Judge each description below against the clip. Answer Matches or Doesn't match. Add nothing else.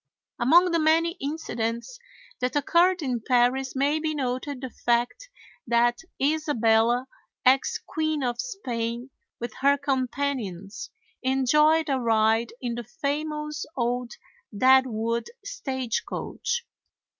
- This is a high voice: Matches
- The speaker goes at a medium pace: Doesn't match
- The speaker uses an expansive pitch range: Doesn't match